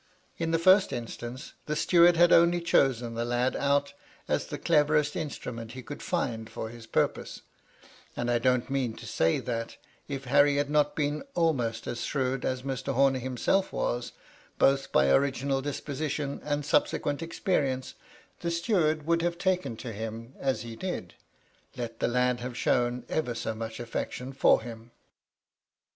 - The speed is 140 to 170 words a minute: Yes, average, 160 wpm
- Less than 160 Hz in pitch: Yes, low, 135 Hz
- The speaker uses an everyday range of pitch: Yes, average, 4.0 semitones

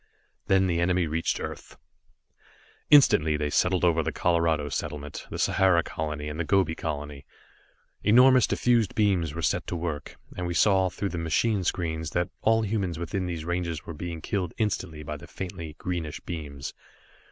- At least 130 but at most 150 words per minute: No, average, 165 wpm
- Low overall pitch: Yes, very low, 85 Hz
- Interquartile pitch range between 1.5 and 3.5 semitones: Yes, average, 3.2 semitones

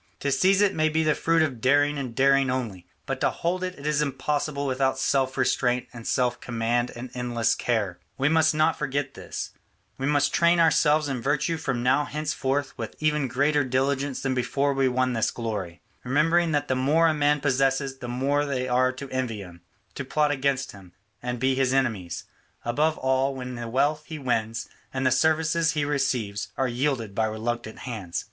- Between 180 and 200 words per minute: Yes, average, 190 wpm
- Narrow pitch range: No, average, 3.2 semitones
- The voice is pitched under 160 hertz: Yes, low, 135 Hz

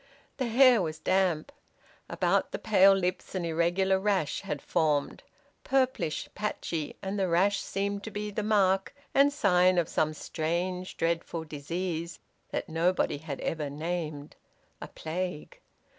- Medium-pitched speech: Yes, medium, 180 Hz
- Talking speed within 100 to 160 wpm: Yes, average, 140 wpm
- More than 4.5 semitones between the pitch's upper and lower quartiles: No, average, 3.7 semitones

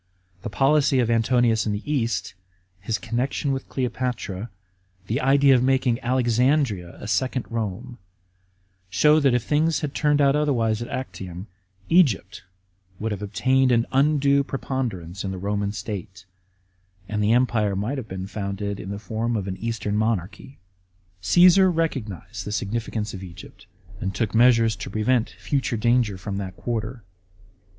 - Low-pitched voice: Yes, low, 115 Hz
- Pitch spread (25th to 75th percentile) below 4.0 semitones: No, average, 4.5 semitones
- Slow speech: No, average, 150 wpm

